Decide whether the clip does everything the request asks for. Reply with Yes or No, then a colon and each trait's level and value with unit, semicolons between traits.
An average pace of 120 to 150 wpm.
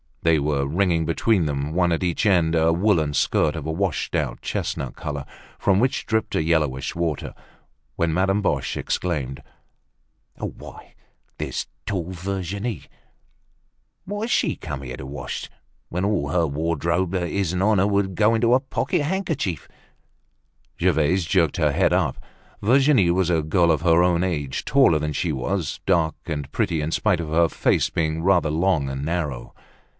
No: average, 165 wpm